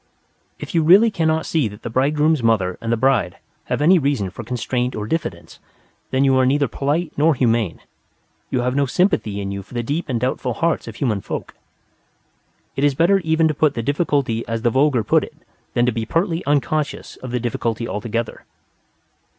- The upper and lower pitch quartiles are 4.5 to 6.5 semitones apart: Yes, average, 5.0 semitones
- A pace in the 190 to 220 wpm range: Yes, average, 195 wpm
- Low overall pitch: Yes, low, 130 Hz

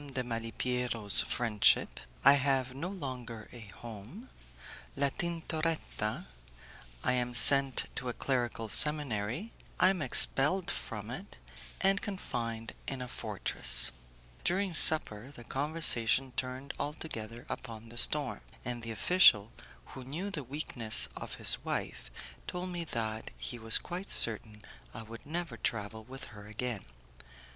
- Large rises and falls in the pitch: No, average, 4.9 semitones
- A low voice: Yes, low, 125 Hz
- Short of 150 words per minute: Yes, slow, 135 wpm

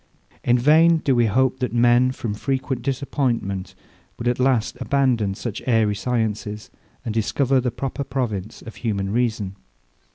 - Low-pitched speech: Yes, low, 120 Hz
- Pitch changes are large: No, average, 3.4 semitones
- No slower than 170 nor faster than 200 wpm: No, average, 150 wpm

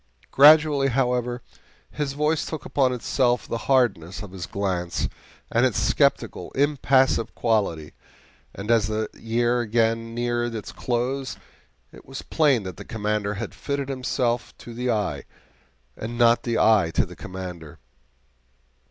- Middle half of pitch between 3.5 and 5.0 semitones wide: Yes, average, 3.8 semitones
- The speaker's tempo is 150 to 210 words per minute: No, average, 140 wpm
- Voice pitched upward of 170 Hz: No, low, 120 Hz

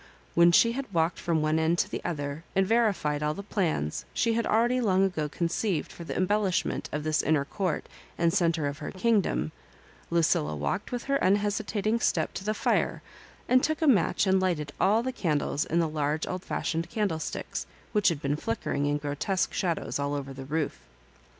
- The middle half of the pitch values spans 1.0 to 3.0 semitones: No, wide, 5.5 semitones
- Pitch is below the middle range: No, medium, 170 Hz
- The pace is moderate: Yes, average, 195 wpm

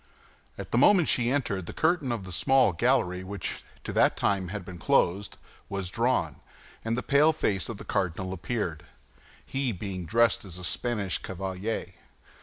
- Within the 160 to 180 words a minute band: Yes, average, 170 wpm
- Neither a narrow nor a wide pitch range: Yes, average, 4.7 semitones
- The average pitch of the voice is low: Yes, low, 100 Hz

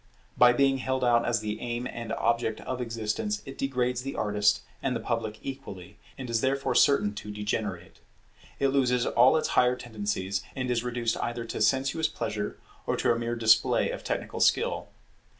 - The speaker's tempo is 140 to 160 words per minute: No, average, 185 wpm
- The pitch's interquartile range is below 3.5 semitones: Yes, average, 3.1 semitones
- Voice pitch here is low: Yes, low, 120 Hz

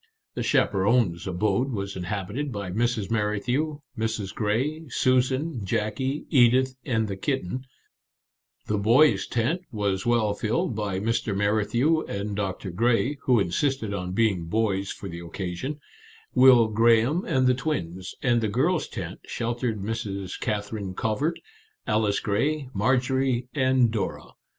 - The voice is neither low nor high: No, low, 115 Hz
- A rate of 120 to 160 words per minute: Yes, slow, 135 wpm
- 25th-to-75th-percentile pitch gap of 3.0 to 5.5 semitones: Yes, average, 4.3 semitones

